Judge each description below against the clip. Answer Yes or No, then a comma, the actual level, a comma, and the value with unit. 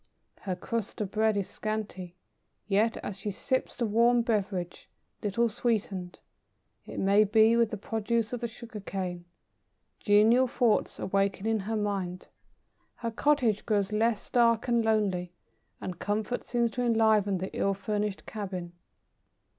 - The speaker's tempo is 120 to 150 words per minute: Yes, average, 145 wpm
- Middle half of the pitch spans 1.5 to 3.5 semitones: Yes, average, 2.8 semitones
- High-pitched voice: Yes, high, 215 Hz